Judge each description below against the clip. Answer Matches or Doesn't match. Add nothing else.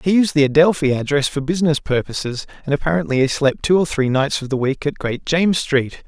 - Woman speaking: Doesn't match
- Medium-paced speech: Doesn't match